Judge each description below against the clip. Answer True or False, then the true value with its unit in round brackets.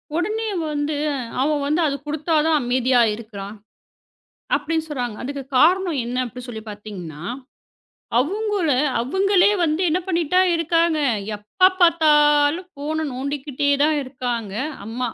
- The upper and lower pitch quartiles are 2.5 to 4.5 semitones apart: False (4.9 semitones)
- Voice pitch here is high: True (295 Hz)